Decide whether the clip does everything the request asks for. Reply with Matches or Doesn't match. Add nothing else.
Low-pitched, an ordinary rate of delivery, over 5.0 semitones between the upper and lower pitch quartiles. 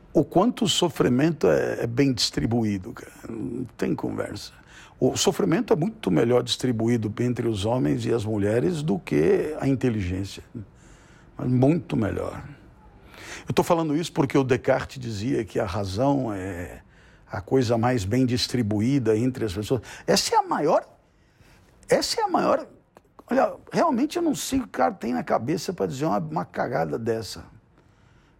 Matches